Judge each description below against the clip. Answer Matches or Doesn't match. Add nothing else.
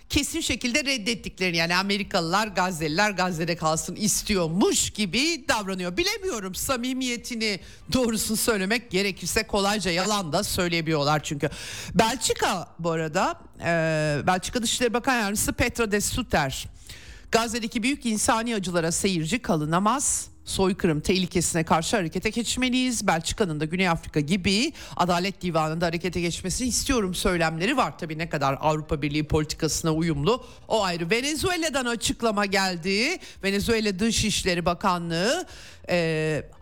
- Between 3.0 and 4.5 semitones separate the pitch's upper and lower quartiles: Doesn't match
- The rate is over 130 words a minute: Doesn't match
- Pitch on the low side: Doesn't match